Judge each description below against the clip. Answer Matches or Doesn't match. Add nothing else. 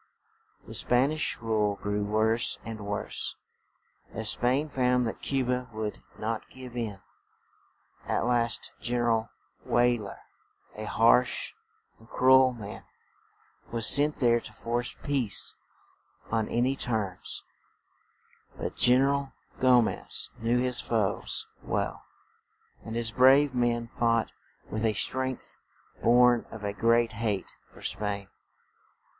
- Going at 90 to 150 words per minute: Matches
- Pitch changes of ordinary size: Doesn't match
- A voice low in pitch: Matches